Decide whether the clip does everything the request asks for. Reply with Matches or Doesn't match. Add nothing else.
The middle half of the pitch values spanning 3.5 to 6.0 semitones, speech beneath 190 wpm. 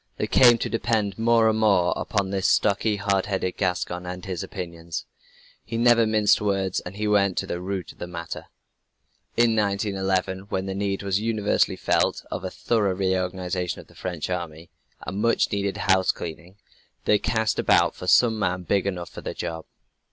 Doesn't match